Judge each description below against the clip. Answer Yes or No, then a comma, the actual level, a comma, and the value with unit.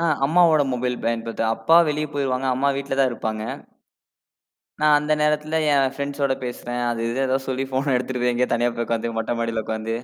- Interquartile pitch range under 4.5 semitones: Yes, average, 3.2 semitones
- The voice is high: No, low, 130 Hz